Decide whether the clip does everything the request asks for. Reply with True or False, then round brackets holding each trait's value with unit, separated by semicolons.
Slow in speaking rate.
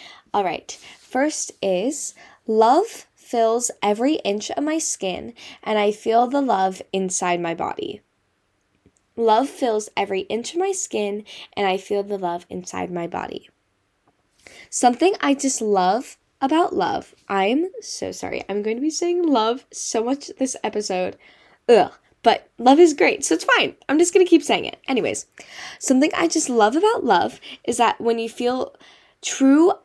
False (165 wpm)